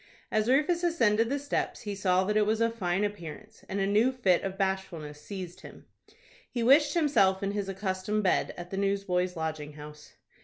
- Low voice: No, high, 195 Hz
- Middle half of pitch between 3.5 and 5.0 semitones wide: Yes, average, 3.8 semitones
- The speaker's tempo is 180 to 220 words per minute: Yes, average, 190 wpm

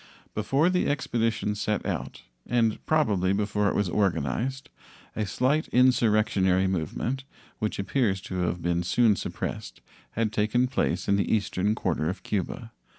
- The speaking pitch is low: Yes, low, 105 Hz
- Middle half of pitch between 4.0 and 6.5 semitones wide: Yes, average, 4.3 semitones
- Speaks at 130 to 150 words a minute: Yes, average, 145 wpm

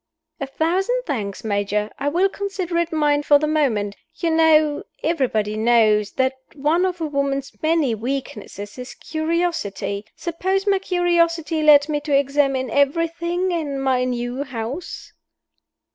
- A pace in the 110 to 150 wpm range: Yes, average, 140 wpm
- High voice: Yes, very high, 290 Hz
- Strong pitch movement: No, average, 5.0 semitones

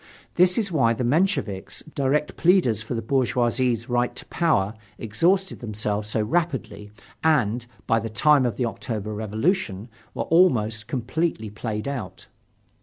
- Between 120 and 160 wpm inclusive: Yes, average, 140 wpm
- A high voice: No, low, 120 Hz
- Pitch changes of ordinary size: No, wide, 6.1 semitones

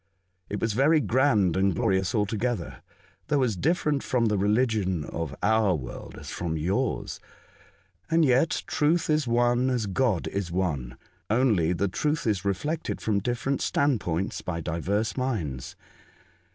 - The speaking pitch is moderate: No, low, 105 Hz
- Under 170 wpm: Yes, average, 140 wpm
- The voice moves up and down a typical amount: No, wide, 6.1 semitones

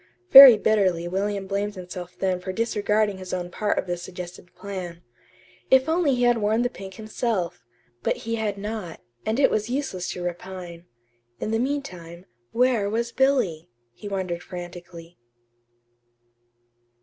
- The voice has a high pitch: Yes, high, 195 Hz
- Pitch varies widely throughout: No, average, 4.1 semitones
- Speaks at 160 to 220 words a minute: No, average, 150 wpm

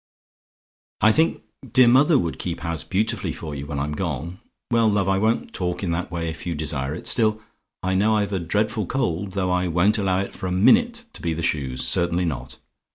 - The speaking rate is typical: No, fast, 215 wpm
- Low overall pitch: Yes, very low, 90 Hz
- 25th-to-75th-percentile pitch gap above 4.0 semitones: Yes, average, 4.4 semitones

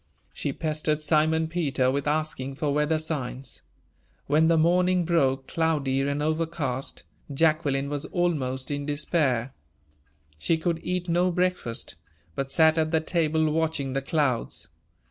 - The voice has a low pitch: No, medium, 155 Hz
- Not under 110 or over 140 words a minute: Yes, slow, 135 wpm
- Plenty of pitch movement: No, average, 3.0 semitones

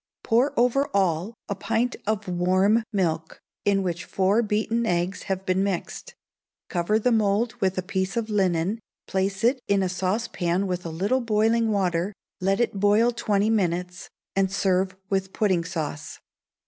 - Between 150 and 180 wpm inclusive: Yes, average, 160 wpm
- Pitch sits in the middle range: No, high, 195 Hz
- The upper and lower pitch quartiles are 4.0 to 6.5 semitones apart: No, average, 3.1 semitones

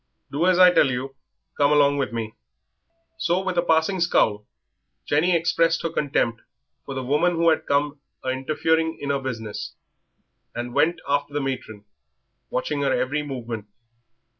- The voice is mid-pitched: Yes, medium, 145 Hz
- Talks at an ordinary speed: Yes, average, 160 wpm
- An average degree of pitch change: Yes, average, 3.9 semitones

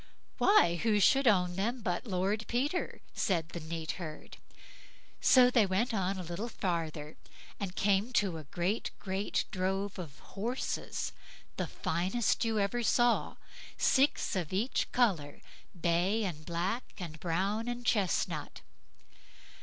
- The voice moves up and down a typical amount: Yes, average, 4.7 semitones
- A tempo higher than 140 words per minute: No, slow, 135 wpm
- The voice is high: Yes, high, 195 Hz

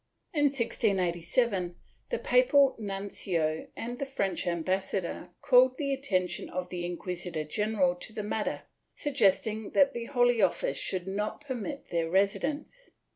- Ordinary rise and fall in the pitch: No, wide, 6.2 semitones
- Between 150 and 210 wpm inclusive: No, slow, 135 wpm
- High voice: Yes, high, 205 Hz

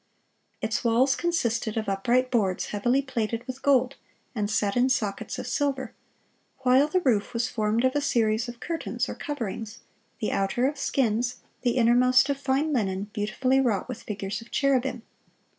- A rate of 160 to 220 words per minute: Yes, average, 165 wpm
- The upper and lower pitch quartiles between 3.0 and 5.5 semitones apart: Yes, average, 3.6 semitones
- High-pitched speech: Yes, high, 245 Hz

